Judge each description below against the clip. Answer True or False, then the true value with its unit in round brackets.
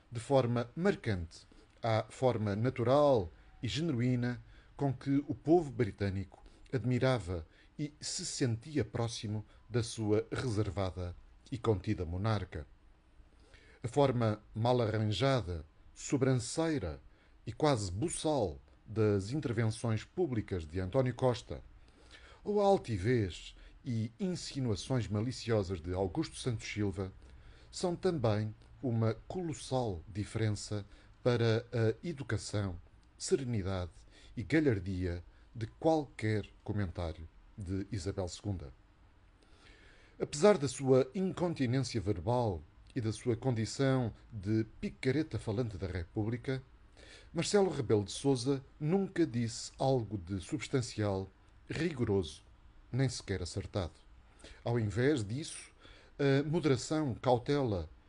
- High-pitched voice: False (110 Hz)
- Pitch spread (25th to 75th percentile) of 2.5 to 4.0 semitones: False (5.0 semitones)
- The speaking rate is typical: False (100 wpm)